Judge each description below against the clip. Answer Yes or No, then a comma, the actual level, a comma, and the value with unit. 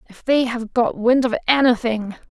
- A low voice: No, high, 240 Hz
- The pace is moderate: Yes, average, 180 wpm